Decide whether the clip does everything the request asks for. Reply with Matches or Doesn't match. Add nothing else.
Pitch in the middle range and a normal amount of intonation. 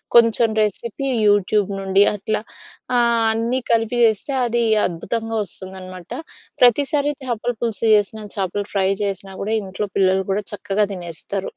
Doesn't match